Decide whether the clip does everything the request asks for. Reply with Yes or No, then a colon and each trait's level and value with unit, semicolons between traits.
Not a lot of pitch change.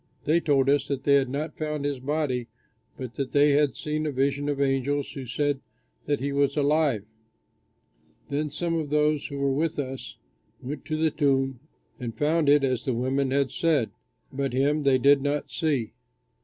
Yes: narrow, 1.9 semitones